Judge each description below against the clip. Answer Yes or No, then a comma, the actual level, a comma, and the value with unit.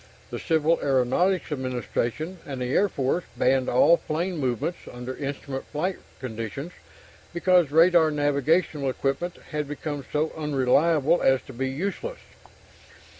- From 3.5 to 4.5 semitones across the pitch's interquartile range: Yes, average, 4.2 semitones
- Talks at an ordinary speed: No, slow, 125 wpm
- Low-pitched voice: No, medium, 150 Hz